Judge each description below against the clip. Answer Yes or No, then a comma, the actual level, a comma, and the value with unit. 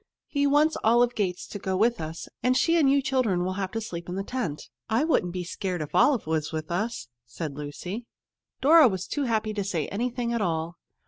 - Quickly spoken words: Yes, fast, 215 wpm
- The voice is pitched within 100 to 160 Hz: No, high, 205 Hz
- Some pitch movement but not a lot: No, wide, 6.0 semitones